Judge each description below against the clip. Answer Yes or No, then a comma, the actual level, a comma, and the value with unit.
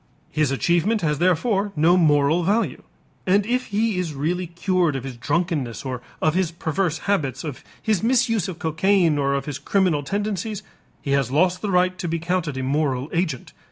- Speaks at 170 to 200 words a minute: Yes, average, 185 wpm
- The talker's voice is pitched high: No, medium, 170 Hz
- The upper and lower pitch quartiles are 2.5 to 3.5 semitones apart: No, average, 4.7 semitones